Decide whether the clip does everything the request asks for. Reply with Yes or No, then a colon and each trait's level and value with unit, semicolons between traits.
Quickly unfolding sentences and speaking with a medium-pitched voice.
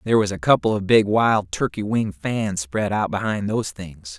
No: fast, 215 wpm; low, 100 Hz